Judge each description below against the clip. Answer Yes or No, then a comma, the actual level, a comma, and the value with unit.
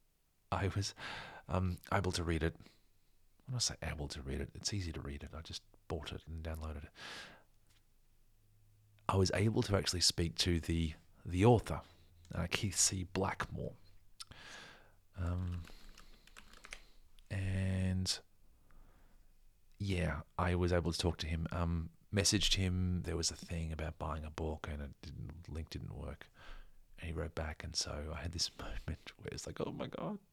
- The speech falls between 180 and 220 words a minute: No, average, 165 wpm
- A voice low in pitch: Yes, very low, 90 Hz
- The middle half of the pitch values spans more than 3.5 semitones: No, average, 3.2 semitones